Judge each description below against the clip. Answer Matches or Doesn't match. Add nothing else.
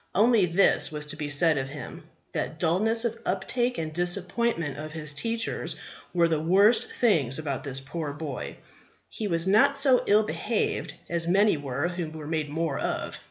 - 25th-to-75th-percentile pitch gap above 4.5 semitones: Matches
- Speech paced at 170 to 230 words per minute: Matches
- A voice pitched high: Doesn't match